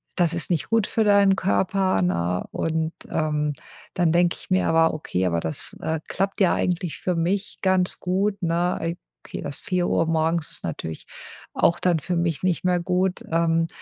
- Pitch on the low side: No, medium, 170 Hz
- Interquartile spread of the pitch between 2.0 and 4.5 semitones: Yes, narrow, 2.6 semitones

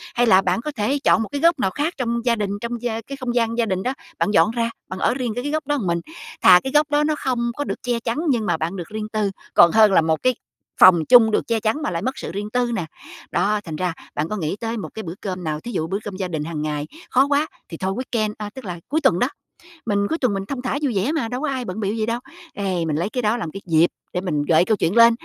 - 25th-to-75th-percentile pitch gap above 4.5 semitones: Yes, average, 5.1 semitones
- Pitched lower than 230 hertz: Yes, high, 220 Hz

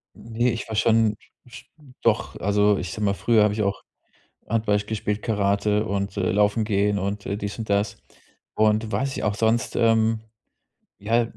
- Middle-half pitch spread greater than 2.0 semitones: No, narrow, 1.7 semitones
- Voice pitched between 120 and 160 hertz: No, low, 105 Hz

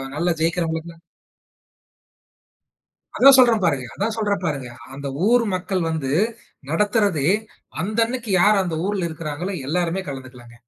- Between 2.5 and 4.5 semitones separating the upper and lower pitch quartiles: No, wide, 5.4 semitones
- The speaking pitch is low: No, medium, 175 Hz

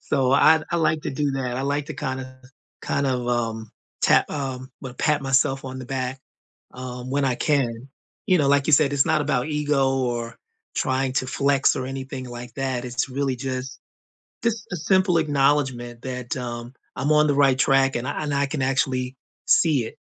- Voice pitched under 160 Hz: Yes, low, 135 Hz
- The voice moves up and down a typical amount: No, narrow, 2.1 semitones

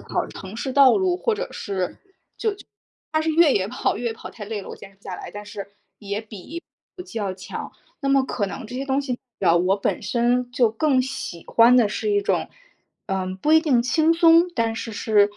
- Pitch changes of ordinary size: No, wide, 5.8 semitones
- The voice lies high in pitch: Yes, high, 235 Hz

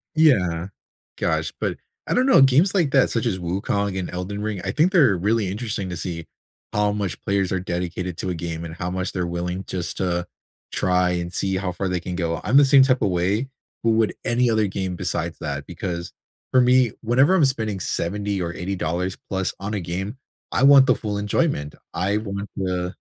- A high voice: No, very low, 95 Hz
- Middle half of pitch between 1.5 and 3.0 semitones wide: No, average, 4.2 semitones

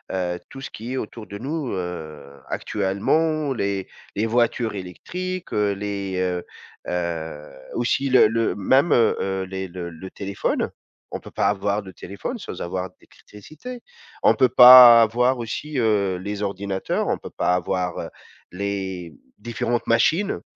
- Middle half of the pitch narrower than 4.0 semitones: No, average, 4.7 semitones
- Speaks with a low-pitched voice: Yes, low, 100 Hz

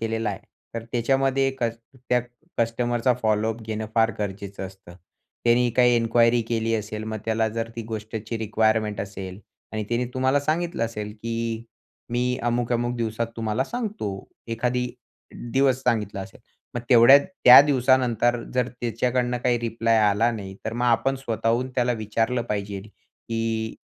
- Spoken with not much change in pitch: Yes, narrow, 2.0 semitones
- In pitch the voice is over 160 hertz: No, low, 115 Hz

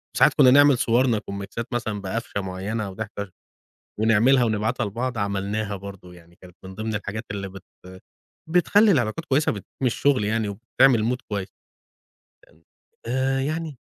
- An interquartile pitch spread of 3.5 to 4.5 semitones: Yes, average, 4.2 semitones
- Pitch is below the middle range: Yes, low, 110 Hz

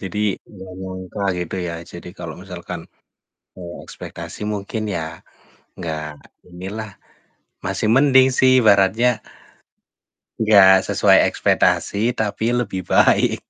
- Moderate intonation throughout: Yes, average, 3.4 semitones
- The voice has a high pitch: No, very low, 95 Hz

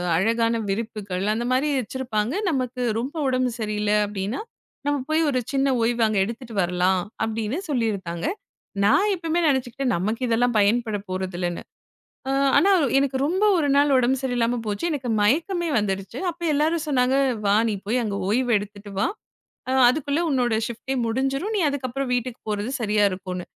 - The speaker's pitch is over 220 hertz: Yes, high, 240 Hz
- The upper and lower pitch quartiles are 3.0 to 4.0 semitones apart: No, average, 4.6 semitones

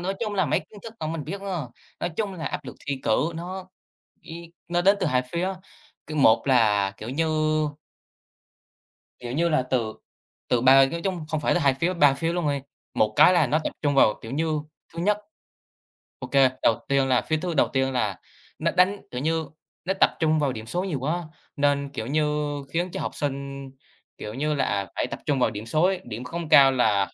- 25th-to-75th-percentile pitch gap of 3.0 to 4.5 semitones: No, average, 4.9 semitones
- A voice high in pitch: No, medium, 150 Hz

